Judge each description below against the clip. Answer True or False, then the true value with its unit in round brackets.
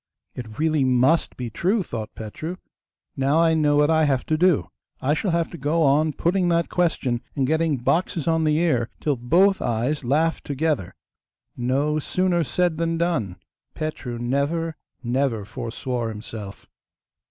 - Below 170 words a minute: True (155 wpm)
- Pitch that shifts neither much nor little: True (4.9 semitones)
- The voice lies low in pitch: False (150 Hz)